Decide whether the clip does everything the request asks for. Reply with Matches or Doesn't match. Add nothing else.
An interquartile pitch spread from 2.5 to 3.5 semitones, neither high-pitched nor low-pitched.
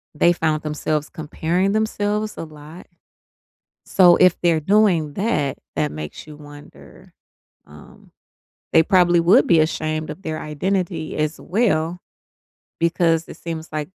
Matches